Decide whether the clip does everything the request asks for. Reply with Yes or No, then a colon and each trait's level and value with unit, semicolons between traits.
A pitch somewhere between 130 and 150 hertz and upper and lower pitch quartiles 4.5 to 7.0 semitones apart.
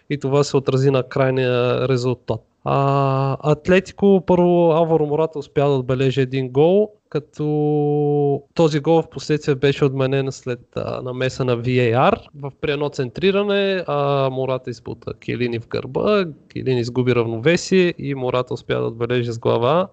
No: medium, 140 Hz; average, 3.2 semitones